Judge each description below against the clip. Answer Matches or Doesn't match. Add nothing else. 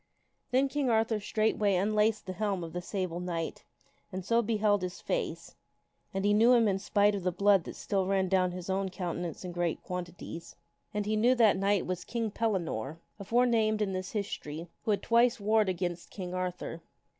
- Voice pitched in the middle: Doesn't match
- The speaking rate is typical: Matches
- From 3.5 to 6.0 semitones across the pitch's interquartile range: Doesn't match